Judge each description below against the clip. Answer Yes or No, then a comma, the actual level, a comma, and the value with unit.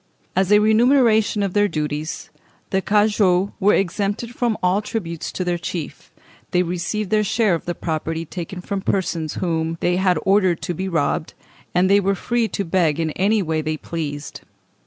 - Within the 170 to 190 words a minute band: Yes, average, 180 wpm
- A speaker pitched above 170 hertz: Yes, medium, 185 Hz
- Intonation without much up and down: No, average, 3.8 semitones